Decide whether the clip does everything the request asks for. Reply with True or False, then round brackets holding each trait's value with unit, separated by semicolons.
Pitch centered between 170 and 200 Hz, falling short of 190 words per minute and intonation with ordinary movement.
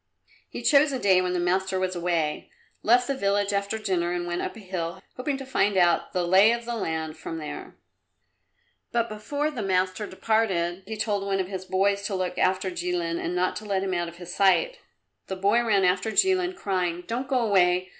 False (190 Hz; 205 wpm; 3.7 semitones)